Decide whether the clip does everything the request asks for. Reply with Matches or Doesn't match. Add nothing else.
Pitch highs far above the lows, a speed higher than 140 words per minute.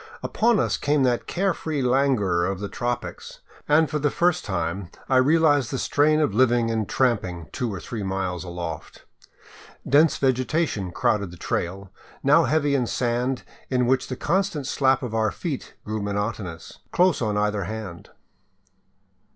Matches